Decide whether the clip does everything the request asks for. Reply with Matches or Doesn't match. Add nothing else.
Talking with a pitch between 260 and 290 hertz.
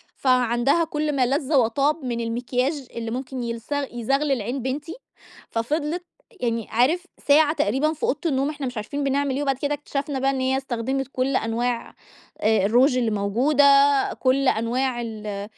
Matches